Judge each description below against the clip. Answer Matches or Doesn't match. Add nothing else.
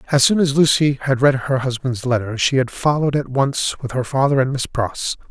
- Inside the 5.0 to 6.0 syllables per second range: Matches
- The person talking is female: Doesn't match